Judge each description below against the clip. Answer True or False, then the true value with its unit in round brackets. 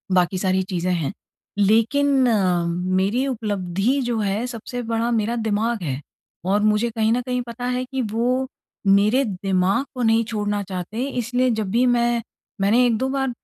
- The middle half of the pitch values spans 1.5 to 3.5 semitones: False (3.9 semitones)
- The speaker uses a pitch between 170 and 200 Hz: False (225 Hz)